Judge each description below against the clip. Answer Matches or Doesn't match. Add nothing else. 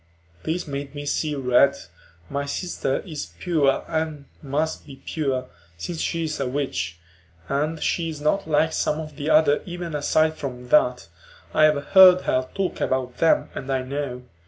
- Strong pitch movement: Doesn't match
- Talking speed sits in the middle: Matches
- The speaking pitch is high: Doesn't match